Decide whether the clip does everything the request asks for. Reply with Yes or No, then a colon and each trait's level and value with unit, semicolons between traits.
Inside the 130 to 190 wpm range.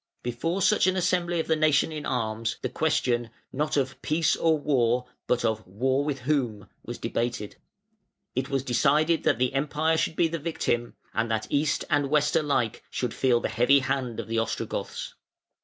Yes: average, 180 wpm